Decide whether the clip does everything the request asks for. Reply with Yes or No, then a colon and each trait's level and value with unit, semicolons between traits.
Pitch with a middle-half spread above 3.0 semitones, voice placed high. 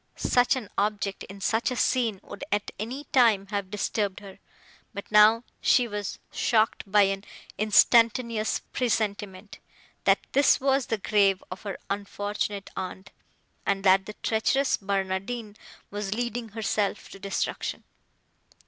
No: narrow, 2.6 semitones; high, 210 Hz